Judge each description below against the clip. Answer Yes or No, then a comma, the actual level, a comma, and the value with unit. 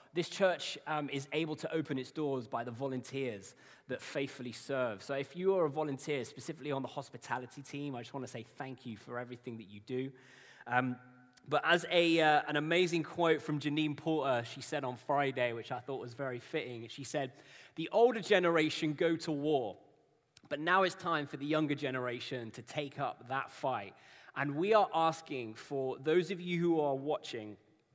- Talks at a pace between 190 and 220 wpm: Yes, average, 195 wpm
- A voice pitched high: No, medium, 140 Hz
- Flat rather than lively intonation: No, average, 4.0 semitones